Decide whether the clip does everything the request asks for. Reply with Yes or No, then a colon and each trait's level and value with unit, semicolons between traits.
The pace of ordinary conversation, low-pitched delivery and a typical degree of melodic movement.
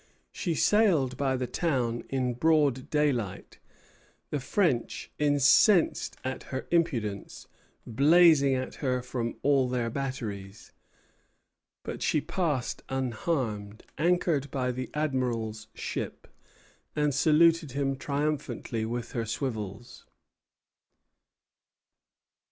No: slow, 100 wpm; low, 130 Hz; average, 4.0 semitones